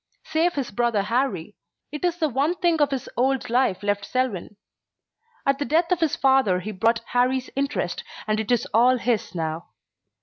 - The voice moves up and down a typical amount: Yes, average, 4.7 semitones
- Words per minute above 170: Yes, average, 180 wpm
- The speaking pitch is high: Yes, very high, 250 Hz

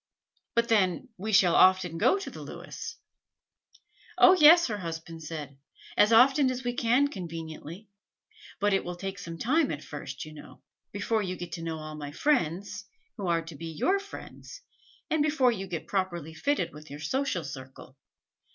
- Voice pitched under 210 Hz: Yes, medium, 185 Hz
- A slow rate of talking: No, average, 175 wpm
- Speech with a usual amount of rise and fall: No, wide, 7.0 semitones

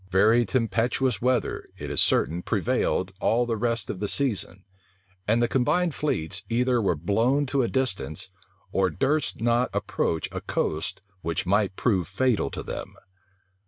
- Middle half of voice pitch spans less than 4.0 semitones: No, average, 4.9 semitones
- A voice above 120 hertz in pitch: No, low, 115 Hz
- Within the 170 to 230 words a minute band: No, average, 155 wpm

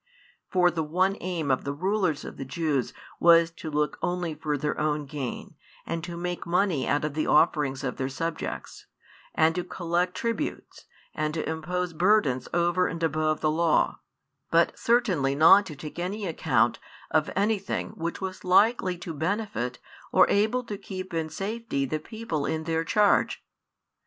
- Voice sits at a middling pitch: Yes, medium, 165 Hz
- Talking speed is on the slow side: No, average, 165 wpm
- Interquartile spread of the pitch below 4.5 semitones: Yes, average, 3.4 semitones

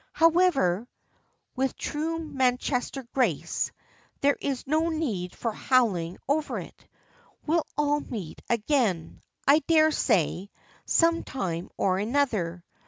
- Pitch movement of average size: No, wide, 7.7 semitones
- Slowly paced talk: Yes, slow, 105 wpm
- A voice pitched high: Yes, very high, 260 Hz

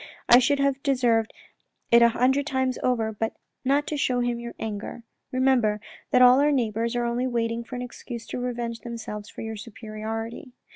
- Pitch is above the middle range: Yes, high, 240 Hz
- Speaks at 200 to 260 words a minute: No, average, 185 wpm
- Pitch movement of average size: No, narrow, 2.2 semitones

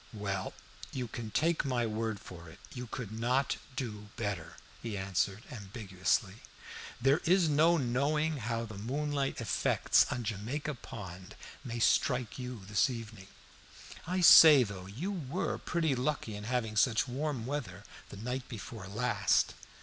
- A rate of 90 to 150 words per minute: Yes, average, 145 wpm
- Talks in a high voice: No, low, 115 Hz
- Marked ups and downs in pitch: No, average, 4.8 semitones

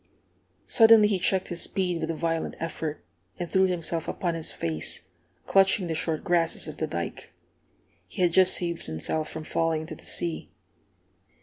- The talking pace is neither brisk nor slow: Yes, average, 170 wpm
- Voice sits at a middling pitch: Yes, medium, 170 Hz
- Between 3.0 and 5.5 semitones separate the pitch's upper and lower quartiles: No, narrow, 2.5 semitones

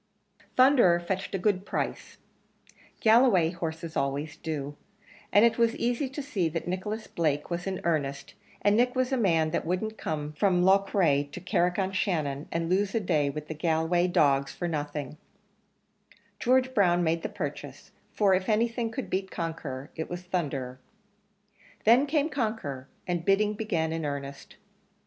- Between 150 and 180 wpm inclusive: Yes, average, 160 wpm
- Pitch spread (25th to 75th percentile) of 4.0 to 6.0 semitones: Yes, average, 5.2 semitones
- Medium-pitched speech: Yes, medium, 175 Hz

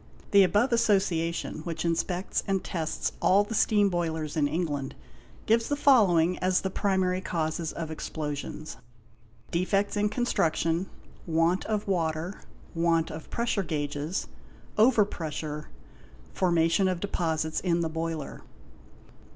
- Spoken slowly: Yes, slow, 125 wpm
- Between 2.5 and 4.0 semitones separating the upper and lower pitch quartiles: Yes, average, 3.6 semitones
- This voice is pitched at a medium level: Yes, medium, 170 Hz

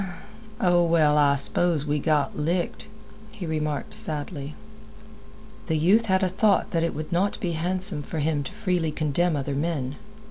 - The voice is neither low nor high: Yes, medium, 160 Hz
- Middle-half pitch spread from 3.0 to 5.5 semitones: Yes, average, 3.3 semitones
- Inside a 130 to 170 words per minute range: Yes, average, 165 wpm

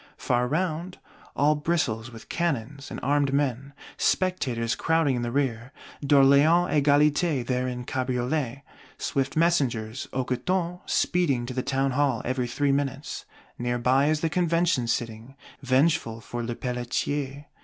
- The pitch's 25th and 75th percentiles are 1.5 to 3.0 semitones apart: No, average, 3.6 semitones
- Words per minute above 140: No, slow, 135 wpm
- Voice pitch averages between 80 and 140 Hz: Yes, low, 135 Hz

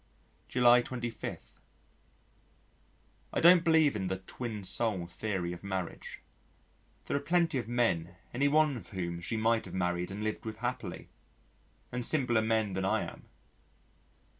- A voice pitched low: Yes, low, 110 Hz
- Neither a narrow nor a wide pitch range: Yes, average, 4.8 semitones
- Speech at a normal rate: Yes, average, 145 wpm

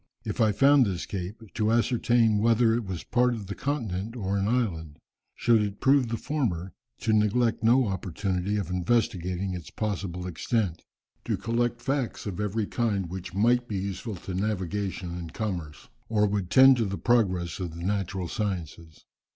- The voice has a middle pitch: No, low, 105 Hz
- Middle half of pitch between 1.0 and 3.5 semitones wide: No, average, 4.0 semitones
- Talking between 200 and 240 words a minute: No, average, 170 wpm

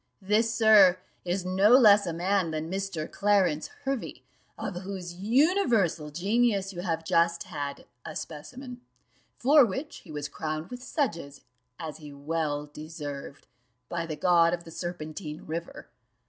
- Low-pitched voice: No, medium, 175 Hz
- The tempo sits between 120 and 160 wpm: Yes, average, 145 wpm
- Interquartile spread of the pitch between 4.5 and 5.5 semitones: Yes, average, 4.8 semitones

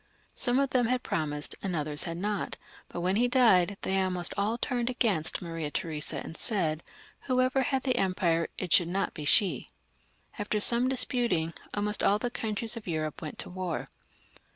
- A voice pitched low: No, high, 195 Hz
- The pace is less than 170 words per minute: No, average, 175 wpm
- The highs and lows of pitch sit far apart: Yes, wide, 6.3 semitones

